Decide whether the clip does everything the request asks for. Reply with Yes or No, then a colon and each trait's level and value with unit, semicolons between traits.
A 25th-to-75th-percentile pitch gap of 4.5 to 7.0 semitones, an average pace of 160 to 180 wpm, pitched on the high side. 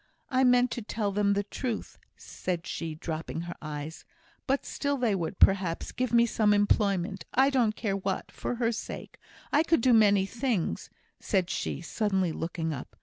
Yes: average, 5.3 semitones; average, 175 wpm; high, 205 Hz